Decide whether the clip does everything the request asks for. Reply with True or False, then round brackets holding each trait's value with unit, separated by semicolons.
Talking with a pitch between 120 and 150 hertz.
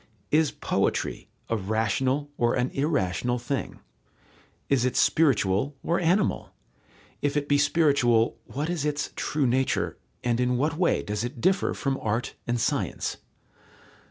True (135 Hz)